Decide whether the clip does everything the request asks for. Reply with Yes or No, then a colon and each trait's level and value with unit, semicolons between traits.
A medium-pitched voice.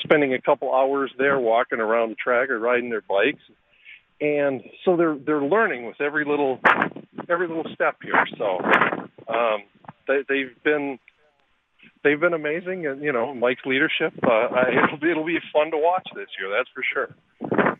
Yes: medium, 145 Hz